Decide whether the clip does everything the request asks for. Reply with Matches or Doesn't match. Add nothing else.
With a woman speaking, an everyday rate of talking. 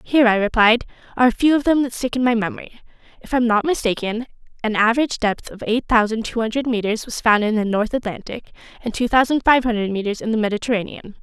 Doesn't match